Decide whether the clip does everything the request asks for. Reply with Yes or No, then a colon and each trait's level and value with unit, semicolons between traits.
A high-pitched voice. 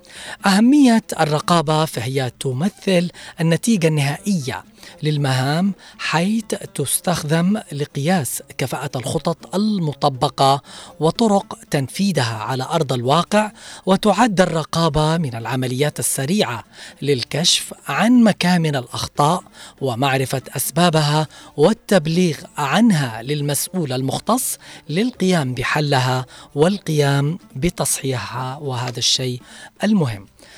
No: medium, 155 Hz